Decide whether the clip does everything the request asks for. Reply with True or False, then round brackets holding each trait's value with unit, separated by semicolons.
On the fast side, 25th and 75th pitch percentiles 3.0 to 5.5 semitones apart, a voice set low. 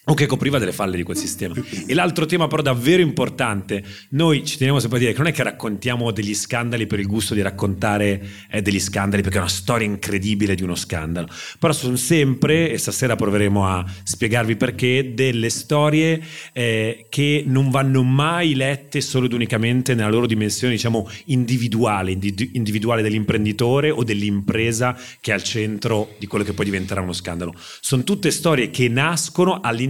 True (185 wpm; 4.7 semitones; 120 Hz)